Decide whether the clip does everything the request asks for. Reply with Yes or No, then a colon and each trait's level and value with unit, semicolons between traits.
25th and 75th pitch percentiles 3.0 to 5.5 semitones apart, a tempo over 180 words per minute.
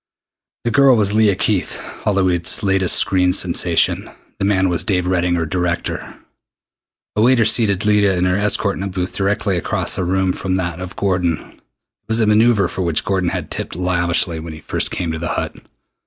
No: narrow, 2.6 semitones; average, 190 wpm